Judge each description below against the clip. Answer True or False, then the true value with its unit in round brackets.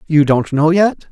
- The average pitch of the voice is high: False (160 Hz)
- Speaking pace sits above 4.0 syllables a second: True (4.3 syllables/s)